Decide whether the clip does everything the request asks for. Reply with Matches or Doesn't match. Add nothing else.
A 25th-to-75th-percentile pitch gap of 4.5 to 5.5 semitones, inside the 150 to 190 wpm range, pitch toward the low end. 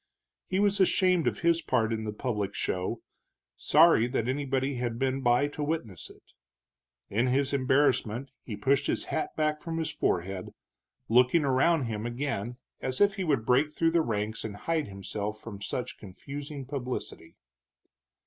Matches